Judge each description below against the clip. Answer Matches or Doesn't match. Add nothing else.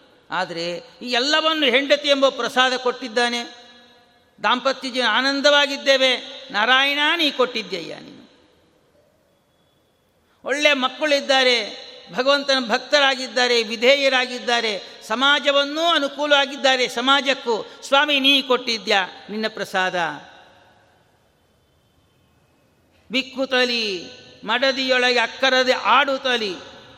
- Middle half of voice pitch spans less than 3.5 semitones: Matches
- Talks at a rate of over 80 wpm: Doesn't match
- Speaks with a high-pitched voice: Matches